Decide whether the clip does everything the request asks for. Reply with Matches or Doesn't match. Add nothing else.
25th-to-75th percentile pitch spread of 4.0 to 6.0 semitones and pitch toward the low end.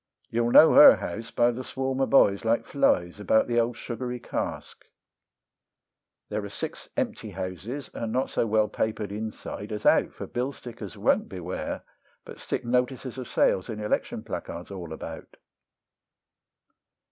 Doesn't match